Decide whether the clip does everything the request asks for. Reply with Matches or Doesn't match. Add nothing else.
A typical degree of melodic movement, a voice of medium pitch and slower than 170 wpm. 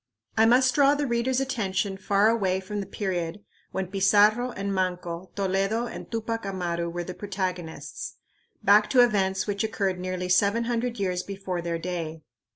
Doesn't match